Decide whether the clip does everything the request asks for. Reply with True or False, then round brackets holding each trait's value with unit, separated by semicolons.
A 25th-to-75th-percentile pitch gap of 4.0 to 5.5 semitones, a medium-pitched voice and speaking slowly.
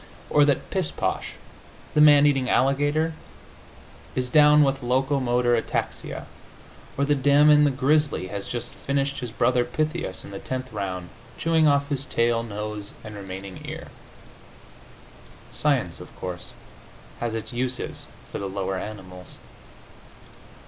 False (5.2 semitones; 125 Hz; 130 wpm)